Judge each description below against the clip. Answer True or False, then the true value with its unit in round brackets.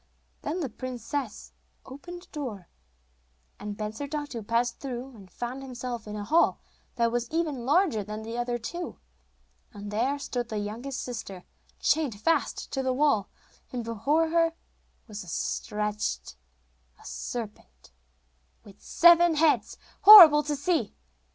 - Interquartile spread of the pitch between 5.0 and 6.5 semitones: True (5.5 semitones)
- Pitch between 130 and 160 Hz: False (245 Hz)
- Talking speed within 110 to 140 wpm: True (135 wpm)